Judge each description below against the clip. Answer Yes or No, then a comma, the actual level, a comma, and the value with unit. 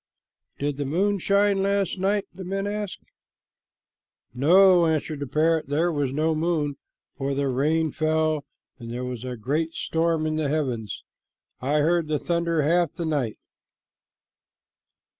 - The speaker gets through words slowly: No, average, 145 wpm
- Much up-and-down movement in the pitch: No, average, 3.5 semitones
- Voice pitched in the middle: Yes, medium, 155 Hz